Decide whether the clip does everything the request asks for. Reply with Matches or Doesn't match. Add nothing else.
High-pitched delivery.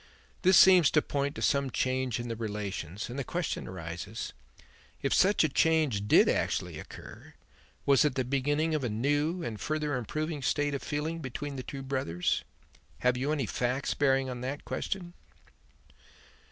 Doesn't match